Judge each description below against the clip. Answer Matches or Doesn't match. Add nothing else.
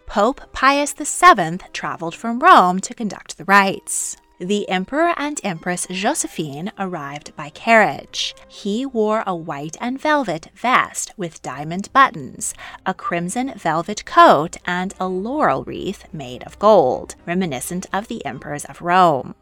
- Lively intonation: Matches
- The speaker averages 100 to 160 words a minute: Matches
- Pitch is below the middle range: Doesn't match